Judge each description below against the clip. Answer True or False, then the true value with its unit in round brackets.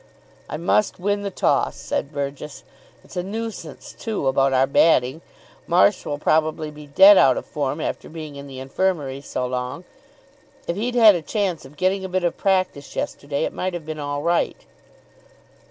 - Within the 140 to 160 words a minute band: False (180 wpm)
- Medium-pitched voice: True (155 Hz)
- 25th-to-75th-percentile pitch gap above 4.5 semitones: True (4.9 semitones)